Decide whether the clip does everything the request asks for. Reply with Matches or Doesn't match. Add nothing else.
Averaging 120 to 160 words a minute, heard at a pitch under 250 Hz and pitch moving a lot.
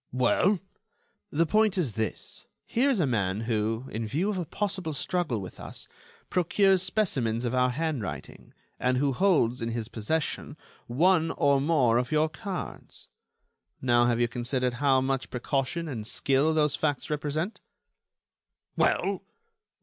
Matches